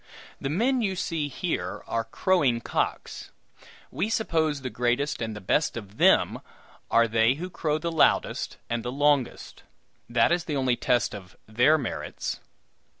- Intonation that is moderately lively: No, wide, 5.8 semitones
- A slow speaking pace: No, average, 155 wpm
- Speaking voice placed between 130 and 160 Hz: Yes, medium, 140 Hz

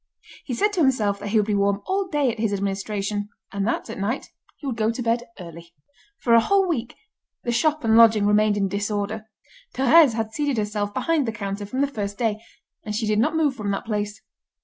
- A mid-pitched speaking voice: No, high, 220 Hz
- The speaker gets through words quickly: Yes, fast, 220 wpm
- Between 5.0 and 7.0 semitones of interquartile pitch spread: No, average, 3.8 semitones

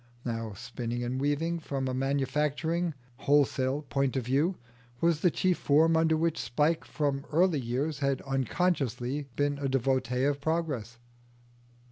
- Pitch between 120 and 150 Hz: Yes, medium, 140 Hz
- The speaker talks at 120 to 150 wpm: Yes, average, 140 wpm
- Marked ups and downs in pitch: No, average, 3.5 semitones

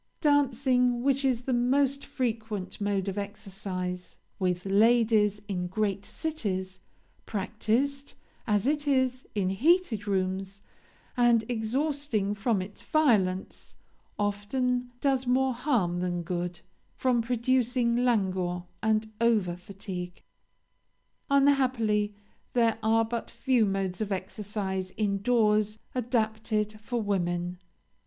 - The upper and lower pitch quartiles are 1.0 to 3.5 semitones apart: No, average, 4.2 semitones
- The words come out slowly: Yes, slow, 110 wpm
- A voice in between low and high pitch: No, high, 215 Hz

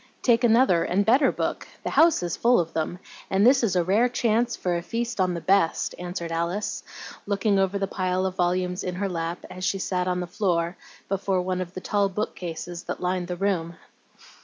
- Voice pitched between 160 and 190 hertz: Yes, medium, 185 Hz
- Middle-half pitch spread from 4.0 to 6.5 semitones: No, narrow, 2.5 semitones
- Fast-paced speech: Yes, fast, 215 wpm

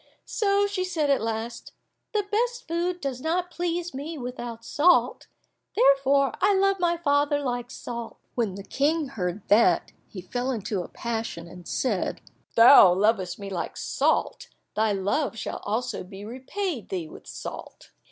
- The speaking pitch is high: Yes, very high, 255 Hz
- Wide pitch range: Yes, wide, 7.8 semitones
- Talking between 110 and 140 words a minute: No, average, 160 wpm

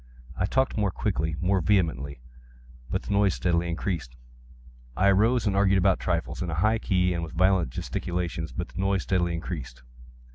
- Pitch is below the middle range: Yes, very low, 90 Hz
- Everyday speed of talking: Yes, average, 170 wpm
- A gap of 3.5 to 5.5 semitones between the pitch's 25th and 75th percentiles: No, average, 2.9 semitones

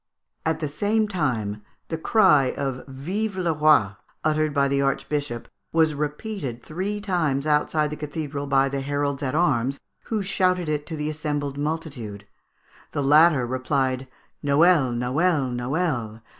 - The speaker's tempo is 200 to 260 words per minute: No, average, 145 wpm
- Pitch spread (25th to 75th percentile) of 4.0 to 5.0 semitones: No, average, 3.2 semitones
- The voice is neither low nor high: Yes, medium, 145 Hz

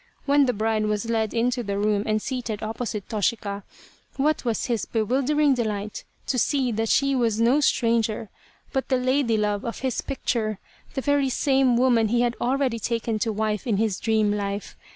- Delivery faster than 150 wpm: Yes, average, 180 wpm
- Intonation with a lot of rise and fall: No, average, 3.2 semitones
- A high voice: Yes, high, 230 Hz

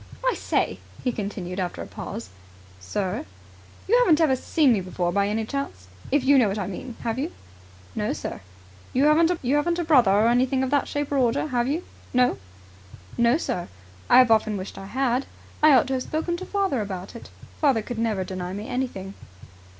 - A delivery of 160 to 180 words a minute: No, average, 195 wpm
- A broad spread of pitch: Yes, wide, 6.1 semitones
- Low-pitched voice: No, high, 245 Hz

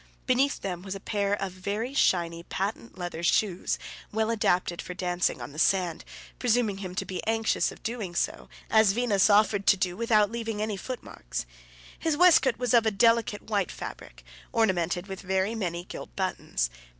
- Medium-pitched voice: No, high, 200 Hz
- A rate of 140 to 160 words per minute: No, average, 175 wpm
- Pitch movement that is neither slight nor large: Yes, average, 3.8 semitones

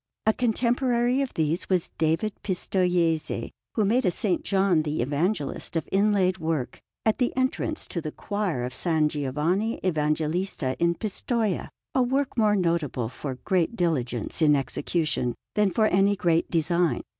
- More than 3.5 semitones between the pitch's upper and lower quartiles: Yes, wide, 5.4 semitones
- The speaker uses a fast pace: No, average, 150 wpm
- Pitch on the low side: No, medium, 175 Hz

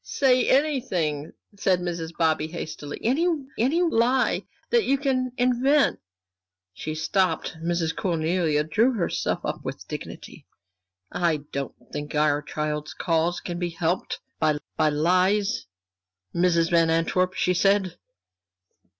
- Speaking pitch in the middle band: Yes, medium, 175 Hz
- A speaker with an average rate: No, slow, 125 wpm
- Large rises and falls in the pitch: Yes, wide, 6.6 semitones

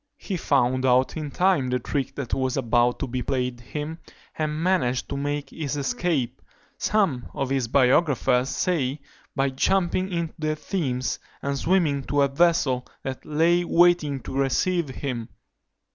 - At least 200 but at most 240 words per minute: No, average, 155 wpm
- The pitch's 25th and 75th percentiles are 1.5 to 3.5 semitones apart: No, average, 4.3 semitones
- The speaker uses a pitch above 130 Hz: Yes, medium, 140 Hz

